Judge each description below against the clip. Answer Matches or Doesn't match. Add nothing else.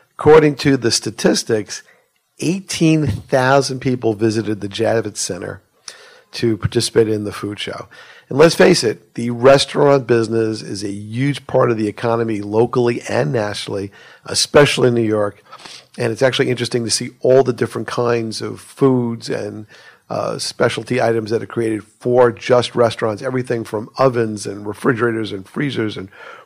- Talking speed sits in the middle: Matches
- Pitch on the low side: Matches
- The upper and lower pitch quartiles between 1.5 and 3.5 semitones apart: Matches